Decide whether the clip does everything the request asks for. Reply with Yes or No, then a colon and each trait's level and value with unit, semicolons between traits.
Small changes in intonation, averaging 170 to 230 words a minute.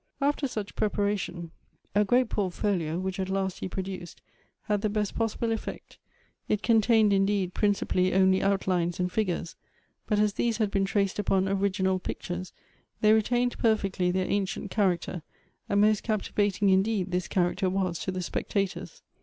No: narrow, 2.2 semitones; average, 155 wpm